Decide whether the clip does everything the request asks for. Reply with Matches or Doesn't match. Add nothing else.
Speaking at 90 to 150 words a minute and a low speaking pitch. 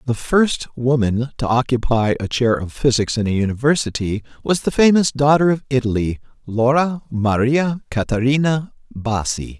Matches